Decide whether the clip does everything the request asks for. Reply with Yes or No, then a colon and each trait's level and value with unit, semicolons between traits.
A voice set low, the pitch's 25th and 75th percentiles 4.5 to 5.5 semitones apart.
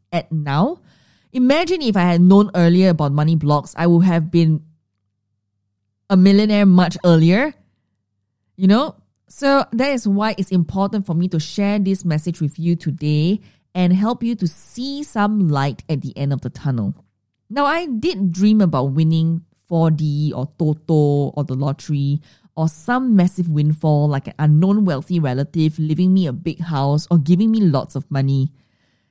No: medium, 165 Hz; average, 4.9 semitones